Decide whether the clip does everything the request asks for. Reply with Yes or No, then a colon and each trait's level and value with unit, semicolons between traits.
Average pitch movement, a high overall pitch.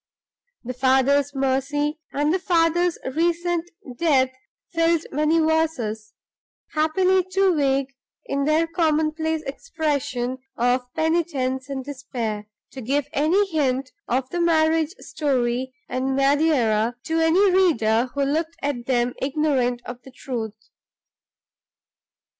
Yes: average, 4.0 semitones; very high, 285 Hz